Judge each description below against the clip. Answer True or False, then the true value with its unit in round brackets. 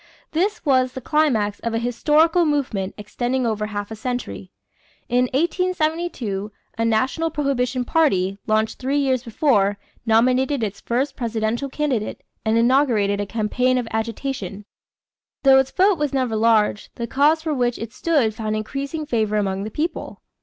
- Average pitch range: True (4.6 semitones)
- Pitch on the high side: True (245 Hz)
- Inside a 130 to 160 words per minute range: True (155 wpm)